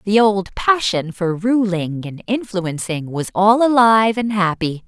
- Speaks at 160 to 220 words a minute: No, average, 150 wpm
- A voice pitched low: No, high, 200 Hz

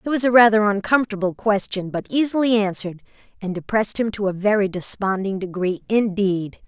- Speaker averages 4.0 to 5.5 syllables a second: No, 5.7 syllables/s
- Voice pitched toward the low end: No, high, 205 Hz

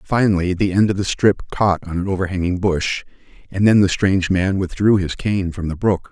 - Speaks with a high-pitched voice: No, very low, 95 Hz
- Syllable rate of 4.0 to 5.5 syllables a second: Yes, 5.3 syllables/s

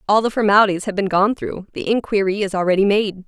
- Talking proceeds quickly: Yes, fast, 220 wpm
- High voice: Yes, high, 200 Hz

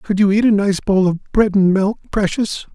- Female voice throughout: No, male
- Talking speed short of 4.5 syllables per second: No, 4.9 syllables/s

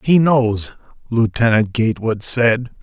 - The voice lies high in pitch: No, low, 120 Hz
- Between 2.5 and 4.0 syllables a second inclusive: Yes, 3.9 syllables/s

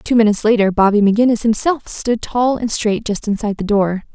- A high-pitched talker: Yes, high, 220 Hz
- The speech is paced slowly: No, fast, 205 wpm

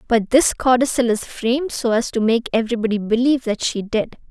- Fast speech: No, average, 195 wpm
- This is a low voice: No, high, 235 Hz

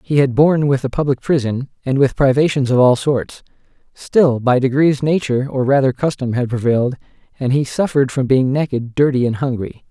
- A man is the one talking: Yes, male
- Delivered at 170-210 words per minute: Yes, average, 190 wpm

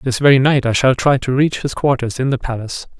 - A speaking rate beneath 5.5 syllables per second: No, 6.0 syllables/s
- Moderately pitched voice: No, low, 130 Hz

